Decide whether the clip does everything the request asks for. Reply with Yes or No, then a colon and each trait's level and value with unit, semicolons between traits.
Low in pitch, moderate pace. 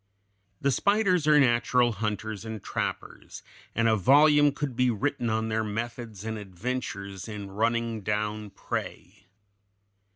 No: low, 115 Hz; slow, 130 wpm